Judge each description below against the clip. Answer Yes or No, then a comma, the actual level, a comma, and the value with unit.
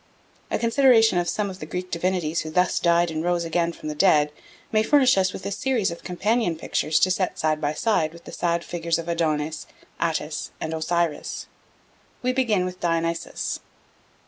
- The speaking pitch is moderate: Yes, medium, 170 Hz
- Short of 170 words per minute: No, average, 185 wpm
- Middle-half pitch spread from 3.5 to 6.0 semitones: No, average, 3.0 semitones